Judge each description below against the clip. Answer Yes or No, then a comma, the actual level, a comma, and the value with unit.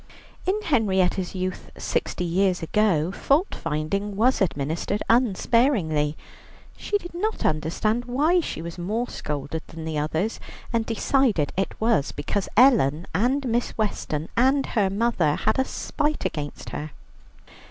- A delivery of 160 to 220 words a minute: No, average, 140 wpm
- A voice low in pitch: No, high, 200 Hz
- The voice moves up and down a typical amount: No, wide, 7.2 semitones